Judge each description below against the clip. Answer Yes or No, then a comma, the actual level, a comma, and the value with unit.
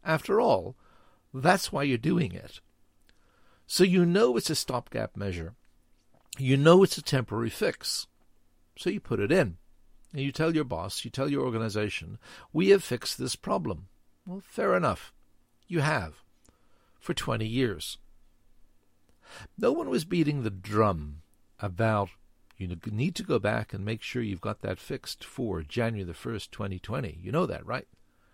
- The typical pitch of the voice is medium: No, low, 105 Hz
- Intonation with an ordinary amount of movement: No, wide, 8.7 semitones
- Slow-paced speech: No, average, 160 wpm